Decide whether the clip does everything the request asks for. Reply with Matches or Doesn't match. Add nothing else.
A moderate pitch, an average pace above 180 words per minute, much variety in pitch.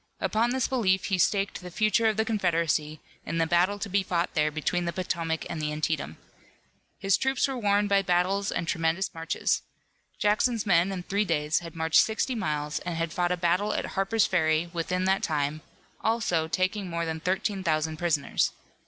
Doesn't match